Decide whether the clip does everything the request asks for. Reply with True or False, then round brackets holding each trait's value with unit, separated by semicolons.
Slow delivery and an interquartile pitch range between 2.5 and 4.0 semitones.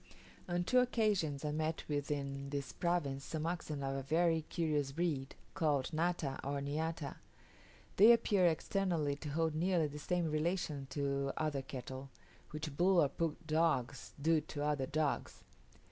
False (155 wpm; 3.3 semitones)